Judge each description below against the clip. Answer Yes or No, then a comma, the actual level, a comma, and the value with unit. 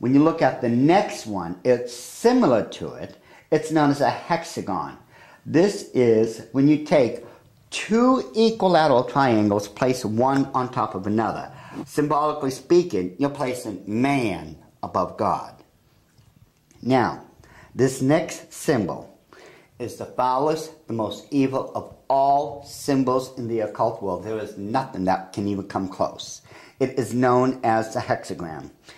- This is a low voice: Yes, low, 130 Hz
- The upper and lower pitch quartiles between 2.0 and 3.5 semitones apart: No, average, 4.6 semitones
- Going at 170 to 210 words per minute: No, average, 140 wpm